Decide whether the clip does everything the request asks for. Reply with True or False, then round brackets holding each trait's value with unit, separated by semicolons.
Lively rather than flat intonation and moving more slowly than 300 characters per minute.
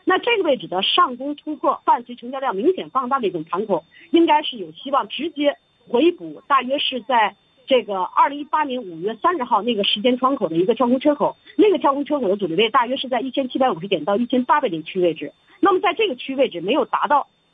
False (6.1 semitones; 360 characters per minute)